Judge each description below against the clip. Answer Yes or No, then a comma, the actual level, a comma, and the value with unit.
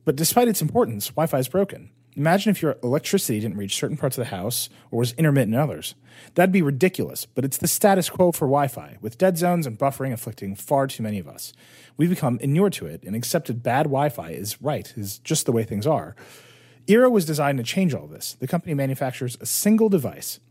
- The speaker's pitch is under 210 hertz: Yes, medium, 140 Hz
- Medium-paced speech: No, fast, 225 wpm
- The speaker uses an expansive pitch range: Yes, wide, 5.9 semitones